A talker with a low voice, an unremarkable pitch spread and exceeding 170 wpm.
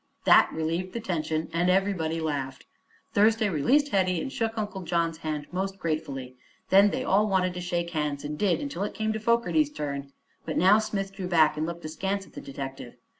No: medium, 180 Hz; average, 4.4 semitones; average, 195 wpm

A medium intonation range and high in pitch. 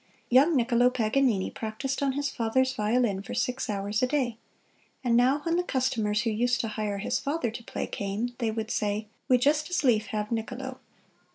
Yes: average, 3.4 semitones; high, 240 Hz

